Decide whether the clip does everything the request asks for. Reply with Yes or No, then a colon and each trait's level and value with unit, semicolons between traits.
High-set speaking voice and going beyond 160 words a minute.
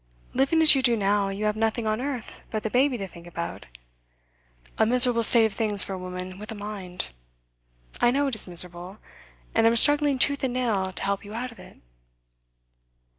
Yes: high, 220 Hz; average, 200 wpm